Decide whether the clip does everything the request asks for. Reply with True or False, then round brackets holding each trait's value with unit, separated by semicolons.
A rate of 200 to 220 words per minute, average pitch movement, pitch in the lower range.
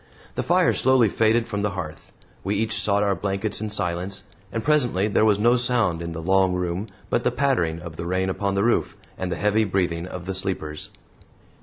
True (205 wpm; 3.5 semitones; 100 Hz)